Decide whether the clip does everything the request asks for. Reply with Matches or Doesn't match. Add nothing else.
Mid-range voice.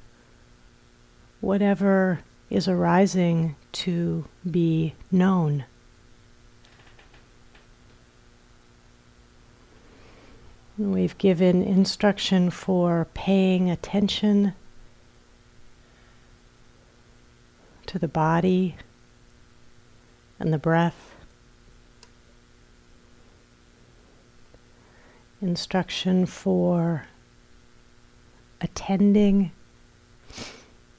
Matches